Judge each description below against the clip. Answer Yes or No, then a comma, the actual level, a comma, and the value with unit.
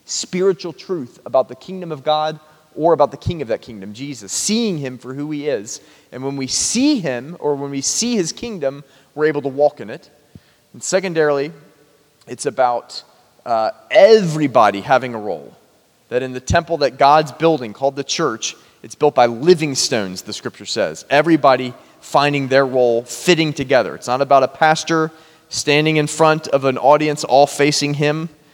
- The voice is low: No, medium, 145 Hz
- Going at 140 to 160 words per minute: No, average, 180 wpm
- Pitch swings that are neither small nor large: Yes, average, 3.0 semitones